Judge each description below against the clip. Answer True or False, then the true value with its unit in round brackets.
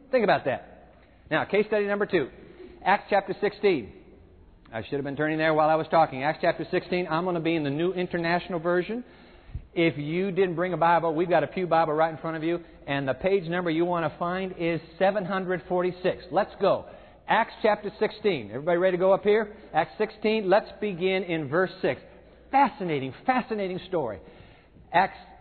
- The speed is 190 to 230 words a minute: True (195 wpm)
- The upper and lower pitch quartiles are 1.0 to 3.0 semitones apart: False (3.4 semitones)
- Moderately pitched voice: True (180 Hz)